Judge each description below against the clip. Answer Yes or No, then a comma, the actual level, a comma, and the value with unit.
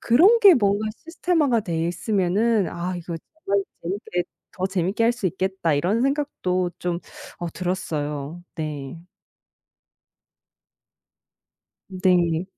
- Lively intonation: No, average, 4.8 semitones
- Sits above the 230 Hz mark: No, medium, 185 Hz